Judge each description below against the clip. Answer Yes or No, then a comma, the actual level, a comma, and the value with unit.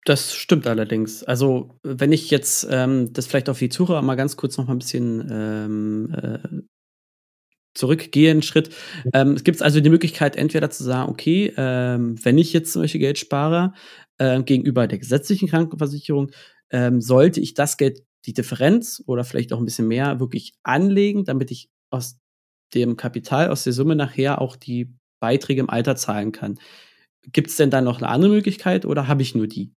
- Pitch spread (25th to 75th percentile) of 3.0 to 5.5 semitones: Yes, average, 3.9 semitones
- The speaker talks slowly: No, average, 180 wpm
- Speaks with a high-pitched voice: No, low, 135 Hz